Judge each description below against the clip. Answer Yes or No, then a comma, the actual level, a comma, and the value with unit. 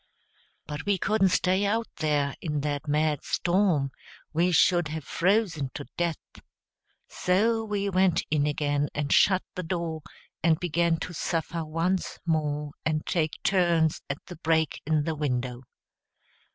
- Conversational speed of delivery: Yes, average, 145 wpm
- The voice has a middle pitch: Yes, medium, 165 Hz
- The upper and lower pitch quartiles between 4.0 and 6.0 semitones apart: No, average, 3.5 semitones